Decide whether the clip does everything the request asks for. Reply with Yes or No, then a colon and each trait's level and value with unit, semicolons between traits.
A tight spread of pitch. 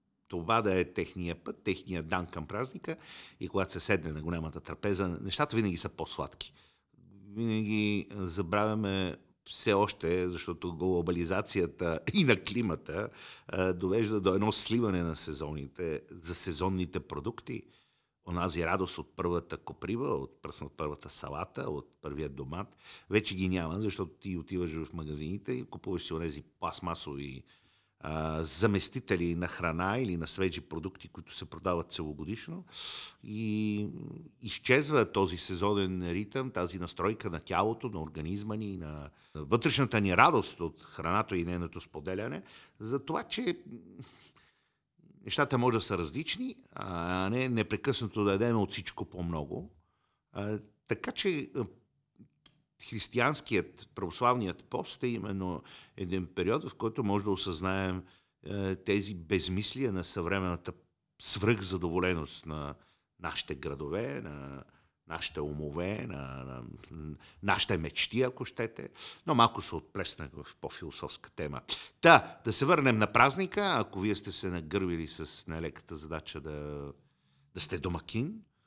No: average, 4.2 semitones